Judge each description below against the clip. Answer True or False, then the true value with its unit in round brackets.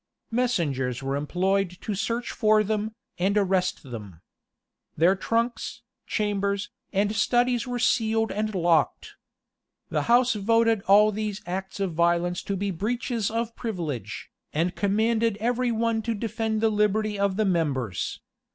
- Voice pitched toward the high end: True (210 Hz)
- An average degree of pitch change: True (3.7 semitones)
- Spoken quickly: False (140 wpm)